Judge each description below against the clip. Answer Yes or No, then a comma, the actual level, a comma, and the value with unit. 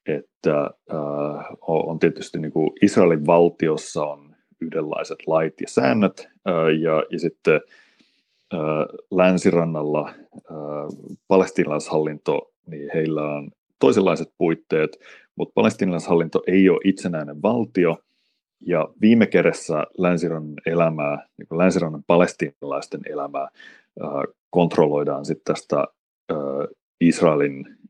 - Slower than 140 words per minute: Yes, average, 100 wpm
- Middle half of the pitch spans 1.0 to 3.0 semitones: Yes, narrow, 2.4 semitones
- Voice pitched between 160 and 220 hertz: No, very low, 80 Hz